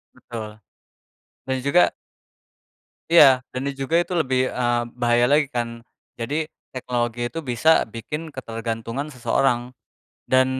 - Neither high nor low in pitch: No, low, 130 Hz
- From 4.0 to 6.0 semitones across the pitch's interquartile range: No, average, 3.0 semitones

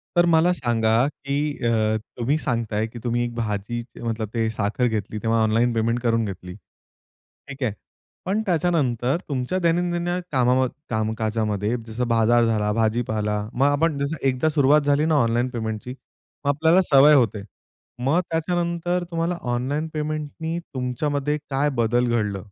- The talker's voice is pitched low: Yes, low, 125 Hz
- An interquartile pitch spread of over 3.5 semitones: Yes, average, 5.0 semitones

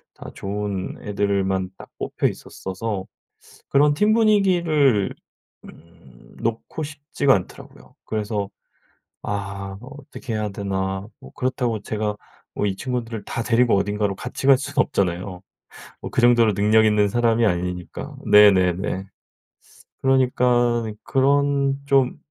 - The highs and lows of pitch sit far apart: No, average, 5.0 semitones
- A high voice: No, low, 110 Hz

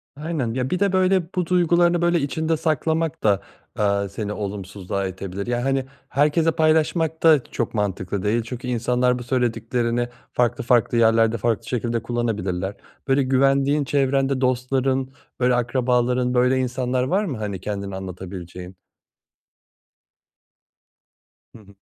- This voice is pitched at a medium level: No, low, 125 Hz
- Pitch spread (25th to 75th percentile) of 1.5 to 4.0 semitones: No, average, 4.6 semitones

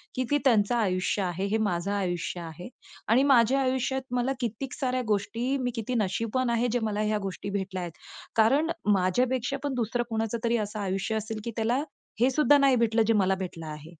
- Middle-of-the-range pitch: No, high, 225 Hz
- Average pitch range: Yes, average, 4.2 semitones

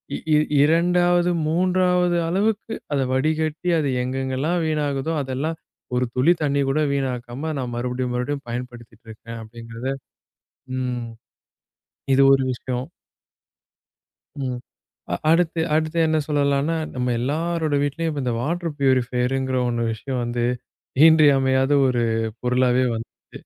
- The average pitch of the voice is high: No, low, 135 Hz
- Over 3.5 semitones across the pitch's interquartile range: Yes, average, 4.1 semitones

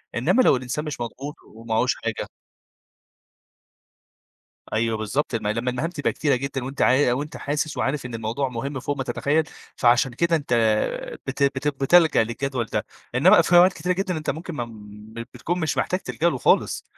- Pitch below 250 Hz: Yes, low, 135 Hz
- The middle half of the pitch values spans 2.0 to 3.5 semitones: No, average, 4.3 semitones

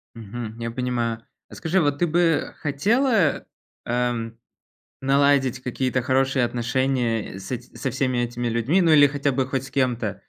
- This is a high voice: No, low, 130 Hz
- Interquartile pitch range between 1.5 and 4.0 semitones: Yes, average, 3.1 semitones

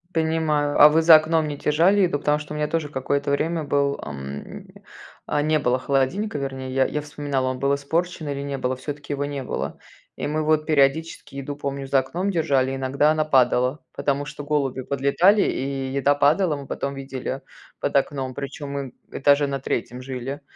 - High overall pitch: No, medium, 140 Hz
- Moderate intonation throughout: No, narrow, 2.0 semitones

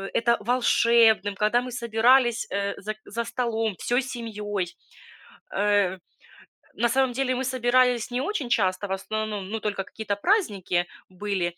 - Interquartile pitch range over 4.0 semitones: No, average, 3.3 semitones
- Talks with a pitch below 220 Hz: No, high, 225 Hz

